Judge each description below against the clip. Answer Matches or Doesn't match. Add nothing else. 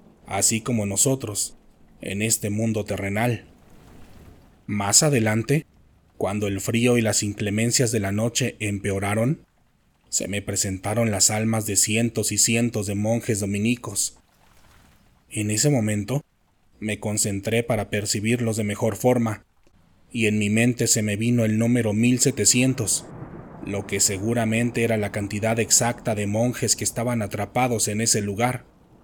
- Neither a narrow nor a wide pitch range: Doesn't match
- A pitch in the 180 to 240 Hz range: Doesn't match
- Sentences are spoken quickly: Doesn't match